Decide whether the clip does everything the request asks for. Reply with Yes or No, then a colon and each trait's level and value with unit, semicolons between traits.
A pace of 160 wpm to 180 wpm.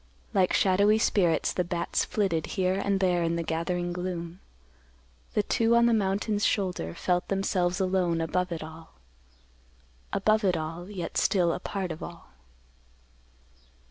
No: average, 145 wpm